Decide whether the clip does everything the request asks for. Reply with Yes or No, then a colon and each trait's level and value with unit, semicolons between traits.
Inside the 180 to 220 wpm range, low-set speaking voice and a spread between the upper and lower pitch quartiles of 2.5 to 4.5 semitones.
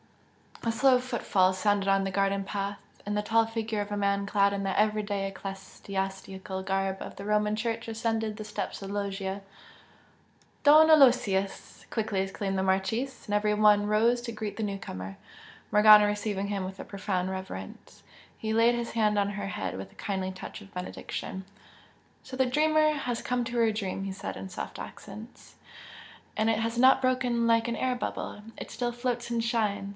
No: average, 185 wpm; high, 210 Hz; average, 2.9 semitones